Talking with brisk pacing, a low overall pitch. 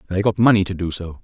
Yes: fast, 290 wpm; very low, 95 Hz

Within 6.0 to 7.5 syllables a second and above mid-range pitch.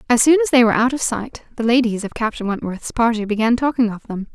Yes: 6.2 syllables/s; high, 235 Hz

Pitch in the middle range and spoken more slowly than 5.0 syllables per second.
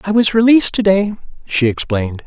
No: medium, 180 Hz; 6.0 syllables/s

